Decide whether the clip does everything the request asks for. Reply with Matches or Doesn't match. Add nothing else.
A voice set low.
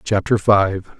Matches